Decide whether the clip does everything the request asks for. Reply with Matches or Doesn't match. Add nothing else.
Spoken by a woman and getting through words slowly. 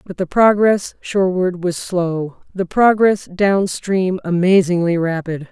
Matches